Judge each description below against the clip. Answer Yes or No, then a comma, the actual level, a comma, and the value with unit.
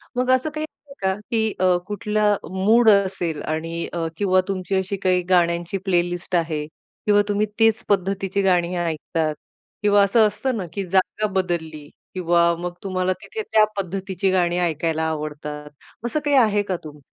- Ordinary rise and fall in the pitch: Yes, average, 3.2 semitones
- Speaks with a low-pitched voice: No, medium, 185 Hz